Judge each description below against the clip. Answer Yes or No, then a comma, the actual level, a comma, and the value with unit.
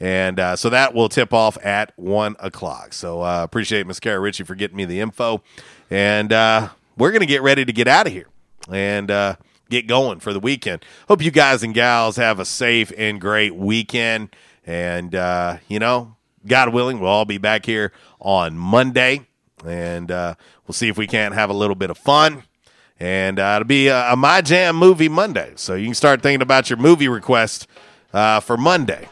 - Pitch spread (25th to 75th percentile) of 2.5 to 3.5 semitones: No, average, 4.5 semitones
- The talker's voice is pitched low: Yes, low, 110 Hz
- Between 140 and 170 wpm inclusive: No, fast, 205 wpm